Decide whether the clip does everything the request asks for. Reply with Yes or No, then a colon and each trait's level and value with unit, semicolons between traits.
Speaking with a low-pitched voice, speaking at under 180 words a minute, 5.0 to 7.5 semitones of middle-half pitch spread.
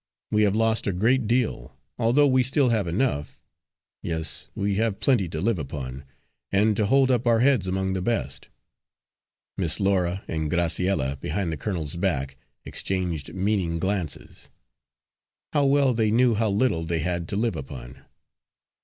Yes: very low, 95 Hz; average, 155 wpm; wide, 5.5 semitones